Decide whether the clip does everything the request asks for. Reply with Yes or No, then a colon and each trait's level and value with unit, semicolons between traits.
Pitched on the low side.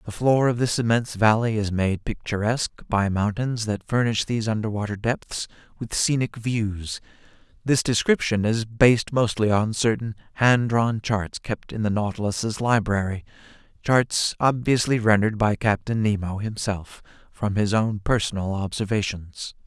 Yes: low, 110 Hz